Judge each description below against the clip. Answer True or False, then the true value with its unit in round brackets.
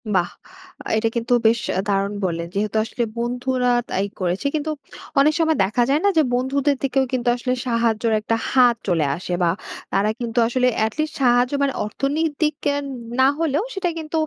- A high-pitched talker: True (245 Hz)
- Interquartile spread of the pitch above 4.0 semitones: True (4.4 semitones)